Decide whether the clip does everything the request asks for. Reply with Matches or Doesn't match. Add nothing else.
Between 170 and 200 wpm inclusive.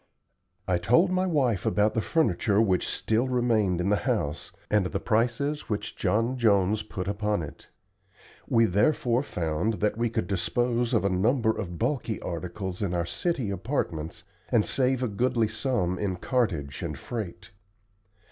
Doesn't match